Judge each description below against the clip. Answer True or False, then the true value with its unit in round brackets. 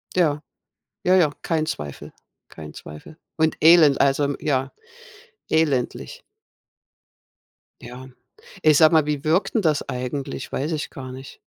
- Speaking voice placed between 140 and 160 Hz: True (145 Hz)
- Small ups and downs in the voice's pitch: False (3.3 semitones)